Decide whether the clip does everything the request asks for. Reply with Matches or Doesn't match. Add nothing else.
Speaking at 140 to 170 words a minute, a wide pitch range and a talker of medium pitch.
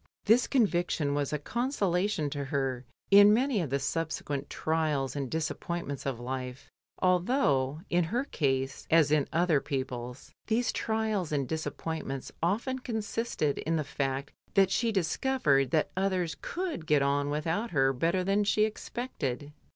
Matches